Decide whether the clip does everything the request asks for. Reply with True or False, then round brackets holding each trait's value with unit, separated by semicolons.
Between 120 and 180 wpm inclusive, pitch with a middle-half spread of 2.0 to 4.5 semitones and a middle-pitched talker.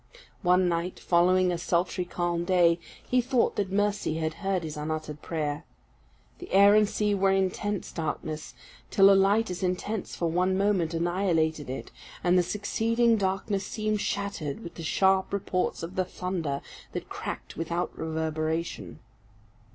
True (150 wpm; 3.2 semitones; 180 Hz)